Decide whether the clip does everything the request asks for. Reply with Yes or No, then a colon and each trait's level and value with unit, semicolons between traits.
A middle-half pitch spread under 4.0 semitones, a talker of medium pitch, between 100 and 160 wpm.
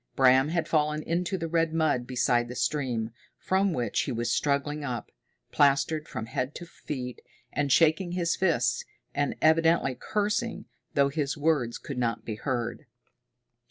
No: average, 4.7 semitones; medium, 145 Hz; average, 155 wpm